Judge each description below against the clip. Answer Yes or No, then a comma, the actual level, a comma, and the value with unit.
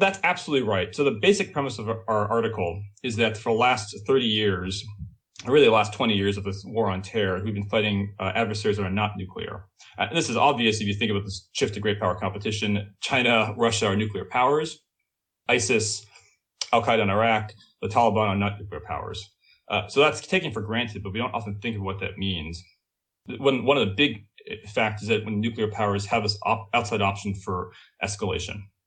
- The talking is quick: Yes, fast, 210 wpm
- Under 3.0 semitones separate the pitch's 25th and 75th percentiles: Yes, narrow, 2.5 semitones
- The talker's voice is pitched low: Yes, low, 105 Hz